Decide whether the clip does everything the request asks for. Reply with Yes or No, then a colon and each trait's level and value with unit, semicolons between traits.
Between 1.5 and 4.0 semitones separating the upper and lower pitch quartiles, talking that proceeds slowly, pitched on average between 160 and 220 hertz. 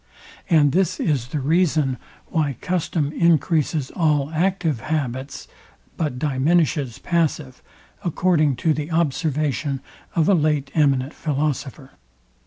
No: average, 3.0 semitones; slow, 110 wpm; medium, 150 Hz